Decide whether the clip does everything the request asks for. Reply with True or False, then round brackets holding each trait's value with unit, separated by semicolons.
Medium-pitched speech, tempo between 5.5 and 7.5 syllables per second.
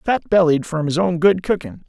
False (170 Hz; 5.1 syllables/s)